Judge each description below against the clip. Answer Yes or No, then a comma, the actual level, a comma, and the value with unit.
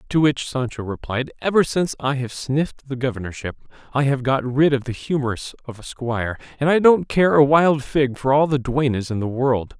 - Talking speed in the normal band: No, fast, 215 wpm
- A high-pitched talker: No, low, 135 Hz